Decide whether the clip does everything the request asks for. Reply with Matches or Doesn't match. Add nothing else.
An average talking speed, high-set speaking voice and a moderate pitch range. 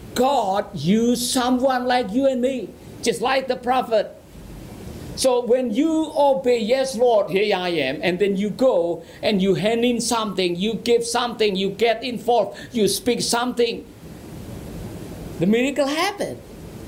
Matches